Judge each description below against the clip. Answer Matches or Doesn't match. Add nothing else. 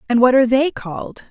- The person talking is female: Matches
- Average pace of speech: Doesn't match